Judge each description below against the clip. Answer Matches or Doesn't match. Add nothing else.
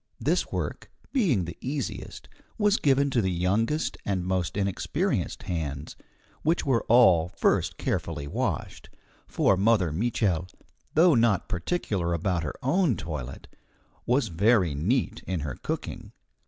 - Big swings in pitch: Matches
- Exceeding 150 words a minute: Doesn't match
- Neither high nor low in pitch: Doesn't match